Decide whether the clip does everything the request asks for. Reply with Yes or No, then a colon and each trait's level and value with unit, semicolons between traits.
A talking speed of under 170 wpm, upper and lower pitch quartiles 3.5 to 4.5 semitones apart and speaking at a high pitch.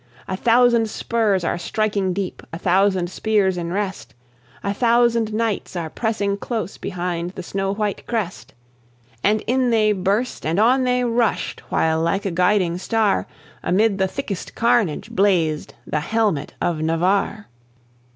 Yes: average, 145 wpm; average, 3.9 semitones; high, 200 Hz